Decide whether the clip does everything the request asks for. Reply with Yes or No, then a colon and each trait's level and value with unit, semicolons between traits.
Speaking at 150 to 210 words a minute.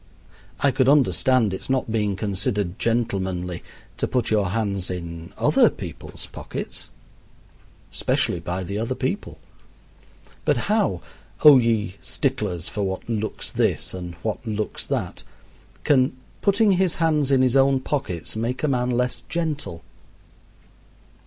No: slow, 135 wpm